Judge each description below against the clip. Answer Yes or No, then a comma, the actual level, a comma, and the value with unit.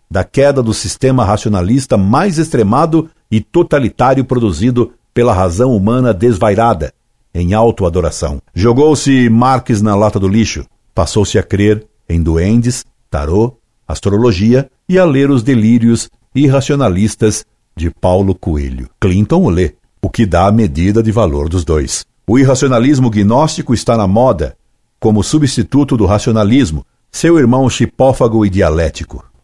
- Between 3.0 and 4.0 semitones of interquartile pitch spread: No, average, 4.9 semitones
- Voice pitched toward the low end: Yes, low, 110 Hz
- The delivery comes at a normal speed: Yes, average, 135 wpm